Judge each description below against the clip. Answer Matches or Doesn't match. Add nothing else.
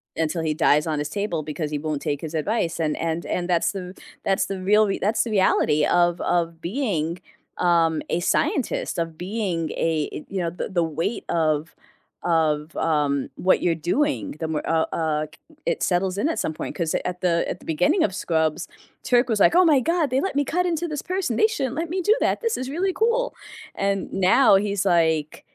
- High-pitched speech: Doesn't match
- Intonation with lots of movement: Matches